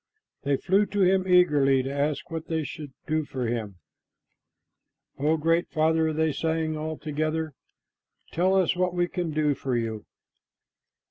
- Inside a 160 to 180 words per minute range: No, average, 150 wpm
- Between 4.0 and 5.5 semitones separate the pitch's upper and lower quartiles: No, average, 2.9 semitones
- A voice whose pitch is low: No, medium, 155 Hz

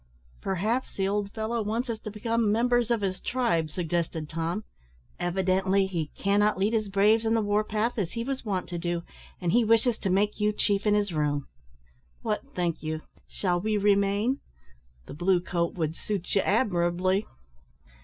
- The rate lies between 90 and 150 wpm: No, average, 175 wpm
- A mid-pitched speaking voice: No, high, 200 Hz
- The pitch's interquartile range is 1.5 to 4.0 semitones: Yes, average, 3.7 semitones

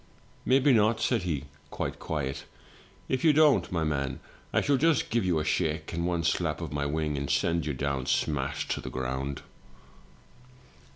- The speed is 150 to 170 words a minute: No, average, 180 wpm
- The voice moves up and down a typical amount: No, wide, 7.9 semitones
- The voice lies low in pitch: Yes, very low, 80 Hz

